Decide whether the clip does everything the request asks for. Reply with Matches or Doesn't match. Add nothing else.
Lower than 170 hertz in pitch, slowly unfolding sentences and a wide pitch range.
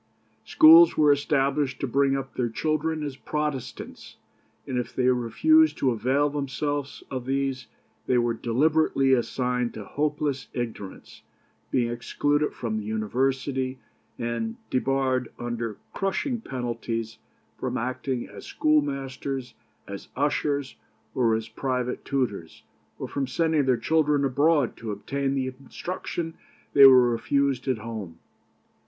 Doesn't match